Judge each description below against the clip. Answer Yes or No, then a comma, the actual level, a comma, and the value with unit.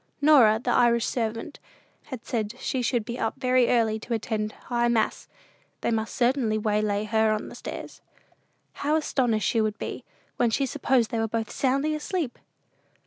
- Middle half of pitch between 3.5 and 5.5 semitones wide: No, average, 2.7 semitones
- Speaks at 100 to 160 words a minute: No, average, 170 wpm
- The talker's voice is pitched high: Yes, high, 235 Hz